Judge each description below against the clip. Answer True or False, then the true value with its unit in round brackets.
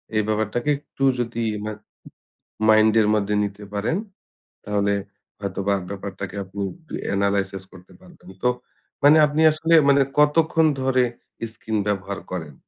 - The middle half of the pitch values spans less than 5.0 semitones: False (5.4 semitones)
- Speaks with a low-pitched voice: True (105 Hz)